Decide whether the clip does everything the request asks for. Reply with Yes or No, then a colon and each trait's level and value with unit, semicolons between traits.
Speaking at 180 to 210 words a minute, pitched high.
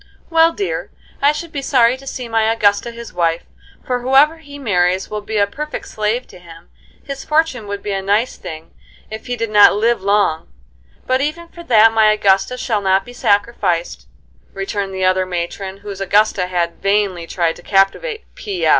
Yes: average, 185 wpm; high, 210 Hz